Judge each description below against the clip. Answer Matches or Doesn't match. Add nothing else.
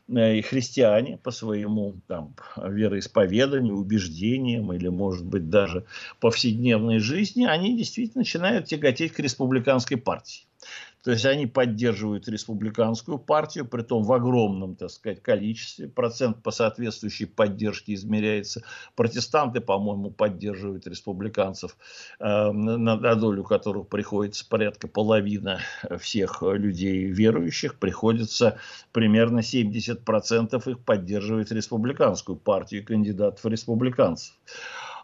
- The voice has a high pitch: Doesn't match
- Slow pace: Matches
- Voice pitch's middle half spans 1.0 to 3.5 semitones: Matches